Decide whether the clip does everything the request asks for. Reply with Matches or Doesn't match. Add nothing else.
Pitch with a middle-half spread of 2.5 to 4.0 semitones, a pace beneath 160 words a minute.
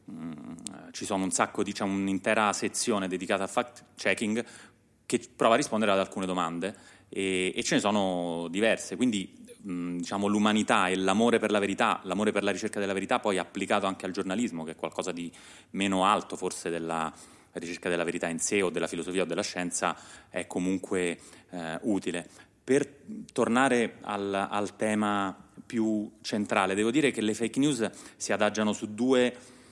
Doesn't match